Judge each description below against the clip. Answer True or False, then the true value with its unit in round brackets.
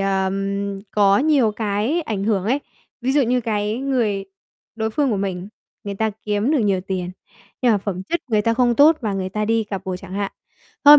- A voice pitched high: True (210 Hz)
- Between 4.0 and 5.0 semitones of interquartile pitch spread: False (3.6 semitones)